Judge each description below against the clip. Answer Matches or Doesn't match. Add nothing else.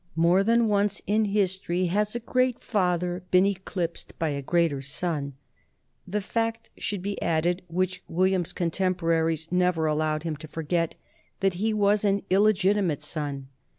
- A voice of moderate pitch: Matches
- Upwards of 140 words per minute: Matches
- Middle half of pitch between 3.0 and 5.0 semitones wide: Matches